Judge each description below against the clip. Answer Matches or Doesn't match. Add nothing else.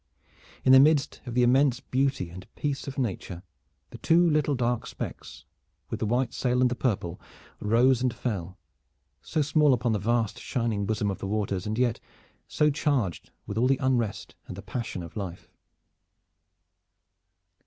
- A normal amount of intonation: Matches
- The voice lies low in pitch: Matches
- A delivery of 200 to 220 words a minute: Doesn't match